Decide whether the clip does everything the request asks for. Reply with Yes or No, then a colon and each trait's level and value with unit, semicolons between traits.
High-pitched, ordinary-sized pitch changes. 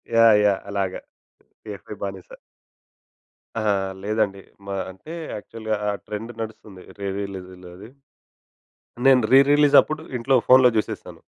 No: low, 105 Hz; average, 3.5 semitones